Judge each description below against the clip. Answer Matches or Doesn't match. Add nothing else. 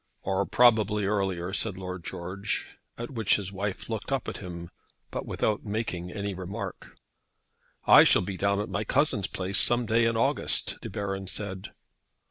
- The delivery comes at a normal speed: Matches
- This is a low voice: Matches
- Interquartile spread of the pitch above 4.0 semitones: Doesn't match